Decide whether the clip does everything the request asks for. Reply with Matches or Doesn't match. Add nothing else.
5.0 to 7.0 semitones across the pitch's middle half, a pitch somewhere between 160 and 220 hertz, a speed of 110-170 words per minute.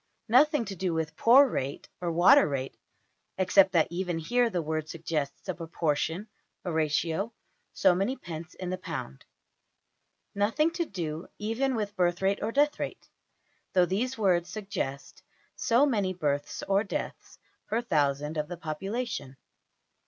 Matches